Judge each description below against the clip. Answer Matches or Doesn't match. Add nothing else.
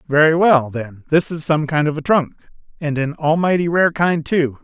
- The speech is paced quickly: Doesn't match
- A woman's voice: Doesn't match